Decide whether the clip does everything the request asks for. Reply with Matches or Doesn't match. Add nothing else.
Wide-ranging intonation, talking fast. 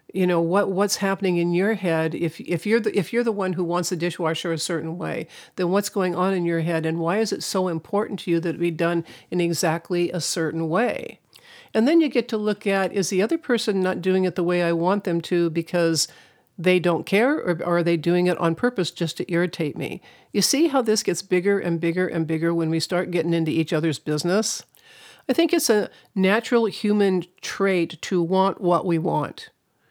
Doesn't match